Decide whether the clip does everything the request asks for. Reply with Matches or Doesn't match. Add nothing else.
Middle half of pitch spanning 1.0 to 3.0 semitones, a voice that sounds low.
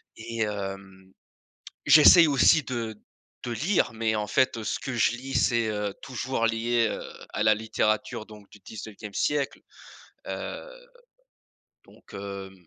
Matches